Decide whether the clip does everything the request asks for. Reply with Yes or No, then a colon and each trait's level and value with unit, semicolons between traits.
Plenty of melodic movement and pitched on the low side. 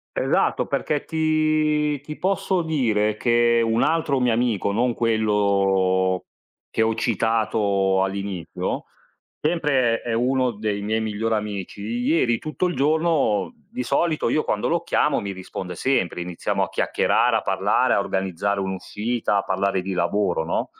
Yes: wide, 6.0 semitones; low, 115 Hz